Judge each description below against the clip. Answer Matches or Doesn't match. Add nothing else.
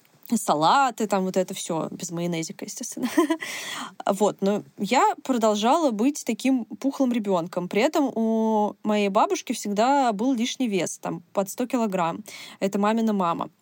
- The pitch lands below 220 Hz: Doesn't match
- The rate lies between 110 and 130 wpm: Doesn't match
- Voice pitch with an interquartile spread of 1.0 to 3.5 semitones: Doesn't match